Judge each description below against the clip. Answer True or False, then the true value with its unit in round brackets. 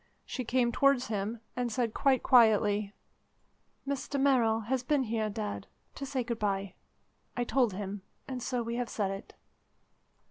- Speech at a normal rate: True (155 wpm)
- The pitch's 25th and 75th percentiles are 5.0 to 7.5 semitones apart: False (3.5 semitones)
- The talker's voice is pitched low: False (235 Hz)